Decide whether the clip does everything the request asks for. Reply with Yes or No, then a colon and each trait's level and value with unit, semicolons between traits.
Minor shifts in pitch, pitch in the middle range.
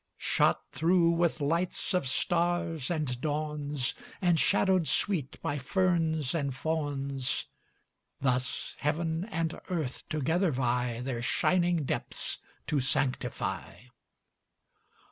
No: average, 4.1 semitones; medium, 155 Hz